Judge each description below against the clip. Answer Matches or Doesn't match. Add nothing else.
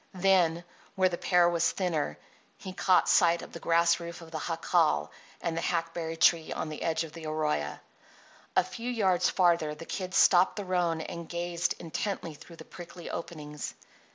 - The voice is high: Doesn't match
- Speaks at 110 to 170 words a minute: Doesn't match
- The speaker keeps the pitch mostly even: Matches